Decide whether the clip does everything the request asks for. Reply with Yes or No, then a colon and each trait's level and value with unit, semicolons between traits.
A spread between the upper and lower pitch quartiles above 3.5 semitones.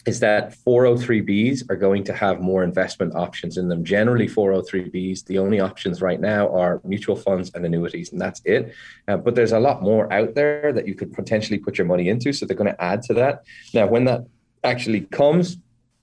Yes: average, 4.5 semitones